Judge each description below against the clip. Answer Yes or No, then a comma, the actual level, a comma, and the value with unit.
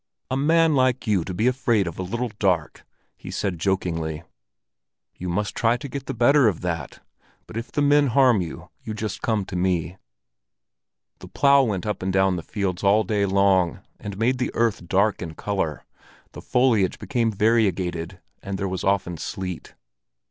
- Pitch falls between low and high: No, low, 100 Hz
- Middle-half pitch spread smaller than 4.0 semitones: No, average, 4.5 semitones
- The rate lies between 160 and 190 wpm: Yes, average, 180 wpm